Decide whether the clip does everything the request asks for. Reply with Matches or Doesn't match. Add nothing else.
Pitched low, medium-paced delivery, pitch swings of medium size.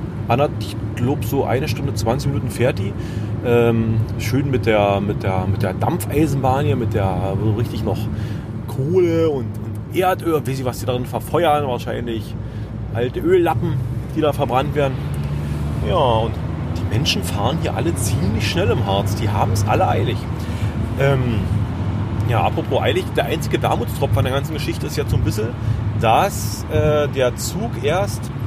Matches